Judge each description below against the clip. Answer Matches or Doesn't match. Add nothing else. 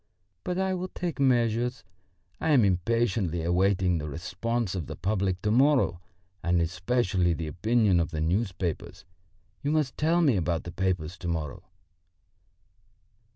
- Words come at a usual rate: Matches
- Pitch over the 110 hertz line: Doesn't match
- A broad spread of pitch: Matches